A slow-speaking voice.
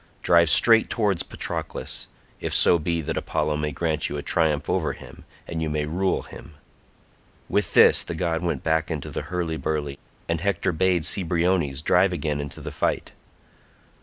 No: average, 170 wpm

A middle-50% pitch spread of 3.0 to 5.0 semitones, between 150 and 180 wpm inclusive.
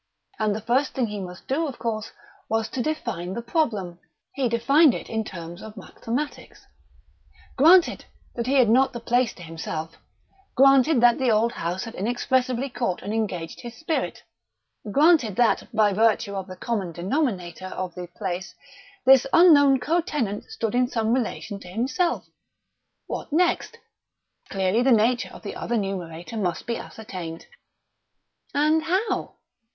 No: wide, 5.5 semitones; average, 155 wpm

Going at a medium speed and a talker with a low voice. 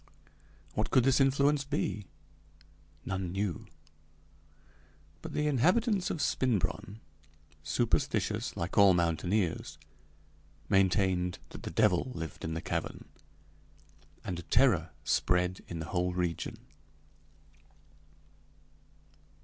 No: slow, 95 wpm; very low, 95 Hz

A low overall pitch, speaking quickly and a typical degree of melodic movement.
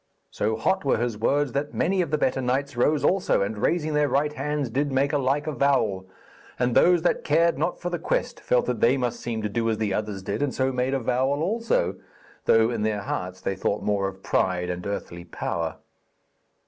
No: low, 130 Hz; fast, 210 wpm; wide, 5.7 semitones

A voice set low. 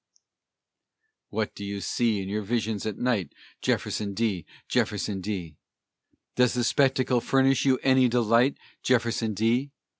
Yes: low, 115 Hz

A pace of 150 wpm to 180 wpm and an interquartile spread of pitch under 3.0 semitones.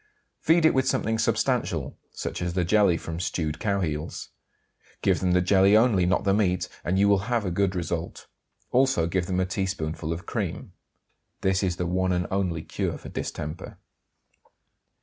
Yes: average, 170 wpm; narrow, 2.5 semitones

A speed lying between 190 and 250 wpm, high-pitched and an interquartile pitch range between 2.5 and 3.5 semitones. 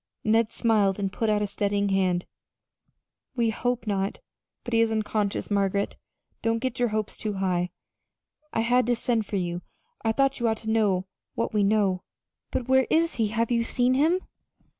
Yes: average, 200 wpm; high, 220 Hz; average, 2.8 semitones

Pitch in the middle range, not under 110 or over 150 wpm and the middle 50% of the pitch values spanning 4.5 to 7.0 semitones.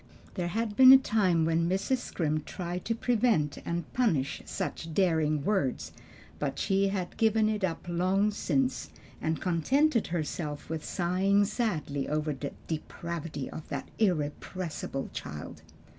Yes: medium, 175 Hz; average, 140 wpm; average, 5.2 semitones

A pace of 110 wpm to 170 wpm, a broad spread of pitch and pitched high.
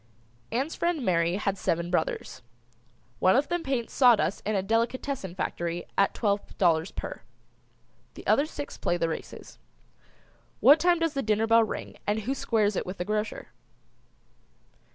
Yes: average, 155 wpm; wide, 6.4 semitones; high, 215 Hz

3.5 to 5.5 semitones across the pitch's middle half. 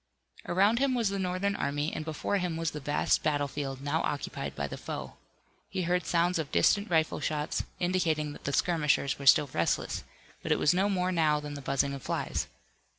Yes: average, 3.8 semitones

